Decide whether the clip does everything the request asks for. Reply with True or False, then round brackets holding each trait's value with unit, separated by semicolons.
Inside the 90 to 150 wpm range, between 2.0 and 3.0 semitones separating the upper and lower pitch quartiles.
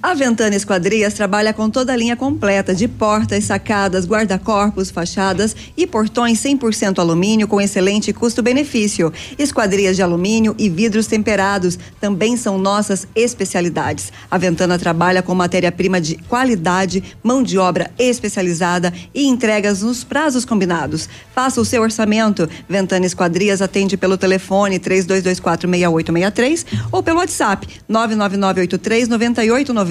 False (120 wpm; 3.5 semitones)